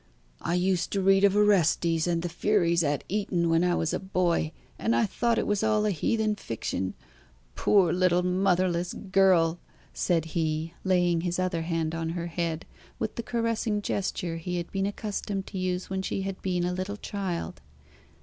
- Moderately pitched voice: Yes, medium, 180 Hz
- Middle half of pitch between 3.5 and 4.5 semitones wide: No, average, 2.7 semitones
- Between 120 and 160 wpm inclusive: No, average, 180 wpm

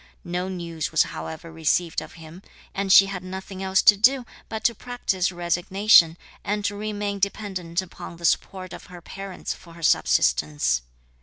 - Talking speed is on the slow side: No, average, 165 wpm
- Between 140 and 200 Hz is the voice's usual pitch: Yes, medium, 185 Hz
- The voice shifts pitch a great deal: No, average, 3.0 semitones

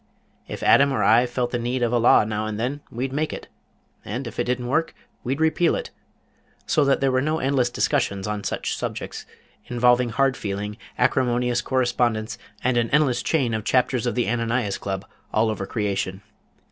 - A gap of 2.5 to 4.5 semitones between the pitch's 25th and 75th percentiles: Yes, average, 3.1 semitones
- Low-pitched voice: Yes, low, 120 Hz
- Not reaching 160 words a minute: No, average, 185 wpm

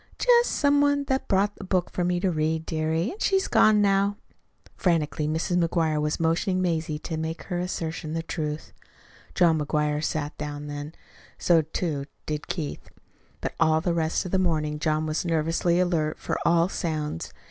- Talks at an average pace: Yes, average, 170 wpm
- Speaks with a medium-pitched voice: Yes, medium, 165 Hz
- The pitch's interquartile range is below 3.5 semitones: Yes, average, 3.0 semitones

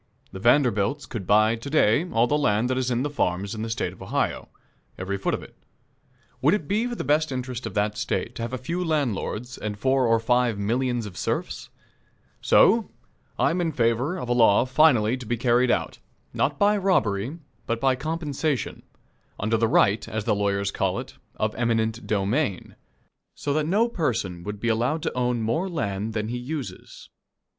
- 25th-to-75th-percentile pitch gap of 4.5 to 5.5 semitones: Yes, average, 5.2 semitones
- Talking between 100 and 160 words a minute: No, average, 190 wpm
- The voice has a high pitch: No, low, 120 Hz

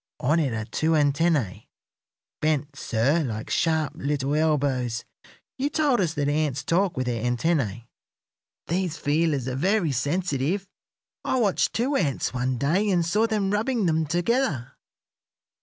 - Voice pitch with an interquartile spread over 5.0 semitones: Yes, wide, 5.4 semitones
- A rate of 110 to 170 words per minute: Yes, average, 140 wpm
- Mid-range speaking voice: Yes, medium, 155 Hz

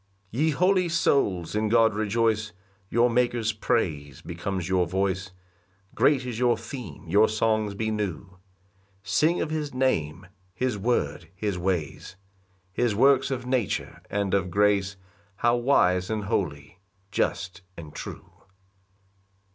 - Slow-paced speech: Yes, slow, 130 wpm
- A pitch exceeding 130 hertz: No, low, 105 Hz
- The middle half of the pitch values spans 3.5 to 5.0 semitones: Yes, average, 4.6 semitones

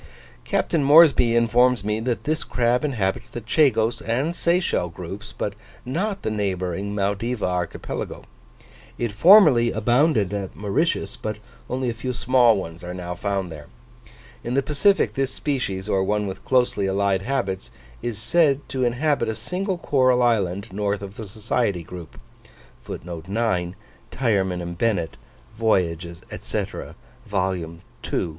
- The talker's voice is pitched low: Yes, low, 115 Hz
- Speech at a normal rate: No, slow, 125 wpm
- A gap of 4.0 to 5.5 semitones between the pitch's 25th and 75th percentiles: Yes, average, 4.8 semitones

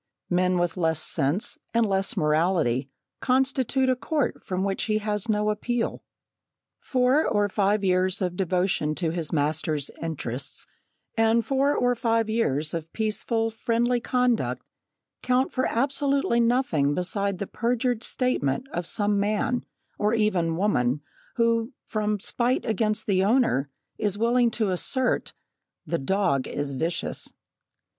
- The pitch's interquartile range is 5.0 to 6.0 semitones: Yes, wide, 5.4 semitones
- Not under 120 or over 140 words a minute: Yes, slow, 135 wpm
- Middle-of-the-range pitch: No, high, 210 Hz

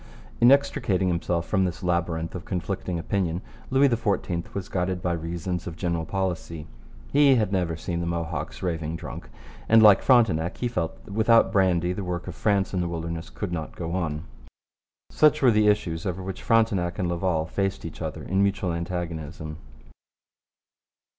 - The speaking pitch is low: Yes, very low, 90 Hz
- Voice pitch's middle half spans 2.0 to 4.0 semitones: Yes, average, 3.0 semitones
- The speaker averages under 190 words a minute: Yes, average, 170 wpm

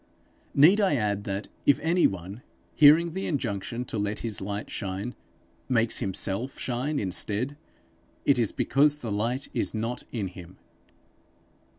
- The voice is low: Yes, low, 115 Hz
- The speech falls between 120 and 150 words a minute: Yes, average, 145 wpm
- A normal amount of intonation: No, wide, 5.7 semitones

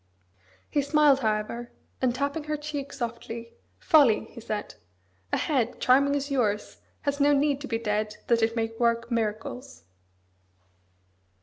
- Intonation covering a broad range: No, average, 3.9 semitones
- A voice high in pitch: Yes, high, 245 Hz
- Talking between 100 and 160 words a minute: Yes, average, 140 wpm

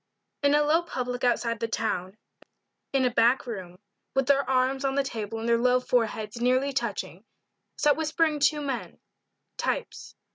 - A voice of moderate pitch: No, very high, 250 Hz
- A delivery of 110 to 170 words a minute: Yes, average, 160 wpm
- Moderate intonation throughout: Yes, average, 3.5 semitones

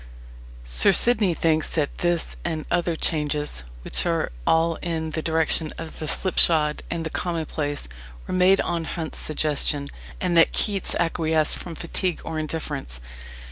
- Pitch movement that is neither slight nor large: No, narrow, 1.9 semitones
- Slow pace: No, average, 145 wpm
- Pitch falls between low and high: Yes, medium, 160 Hz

